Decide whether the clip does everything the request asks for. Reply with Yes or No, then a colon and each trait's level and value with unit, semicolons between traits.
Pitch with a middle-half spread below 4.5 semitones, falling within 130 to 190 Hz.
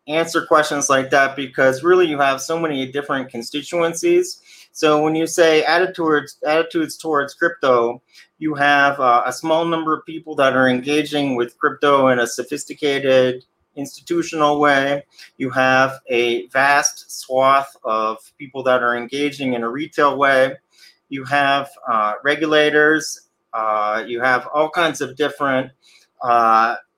Yes: average, 2.9 semitones; medium, 140 Hz